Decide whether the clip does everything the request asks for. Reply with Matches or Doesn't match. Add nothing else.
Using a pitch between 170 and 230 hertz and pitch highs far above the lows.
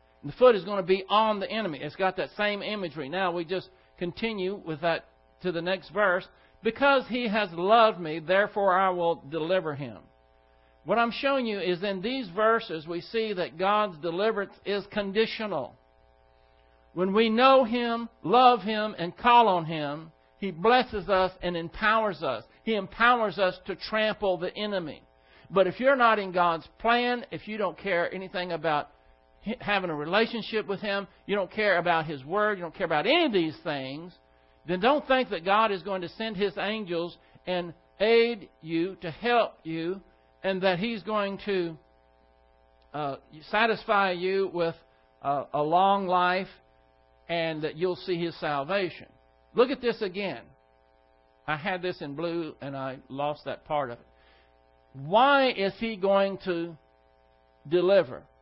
Matches